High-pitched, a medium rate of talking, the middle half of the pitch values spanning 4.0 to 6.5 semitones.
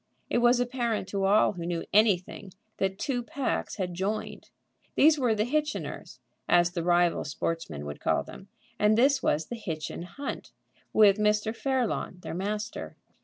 Yes: high, 210 Hz; average, 160 wpm; average, 5.3 semitones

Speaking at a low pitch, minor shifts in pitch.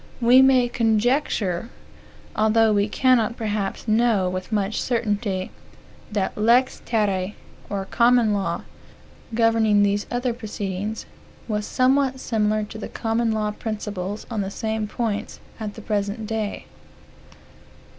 No: high, 215 Hz; narrow, 2.2 semitones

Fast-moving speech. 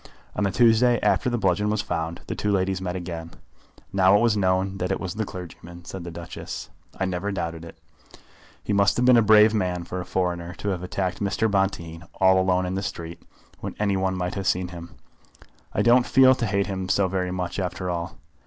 Yes: fast, 220 wpm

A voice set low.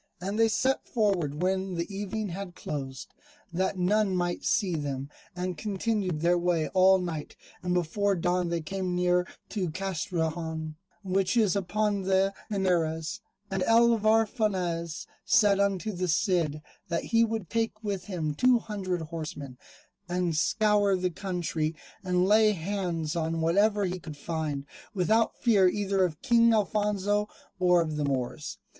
No: medium, 185 Hz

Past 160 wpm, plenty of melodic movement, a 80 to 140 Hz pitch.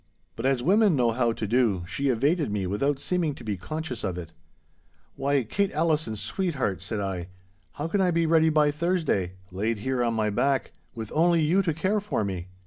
Yes: average, 200 wpm; wide, 7.2 semitones; low, 135 Hz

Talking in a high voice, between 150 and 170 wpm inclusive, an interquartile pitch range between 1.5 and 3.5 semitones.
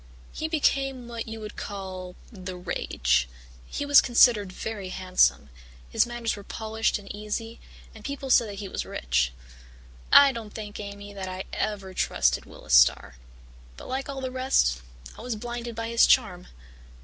No: high, 215 Hz; average, 160 wpm; average, 4.3 semitones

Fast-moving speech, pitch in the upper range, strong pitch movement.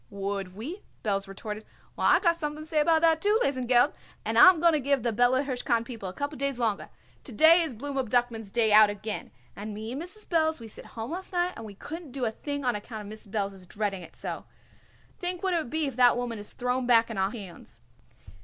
Yes: fast, 240 wpm; high, 245 Hz; wide, 6.3 semitones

